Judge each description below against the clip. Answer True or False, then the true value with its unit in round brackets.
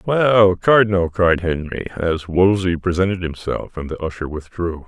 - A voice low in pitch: True (90 Hz)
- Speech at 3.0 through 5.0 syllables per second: True (4.6 syllables/s)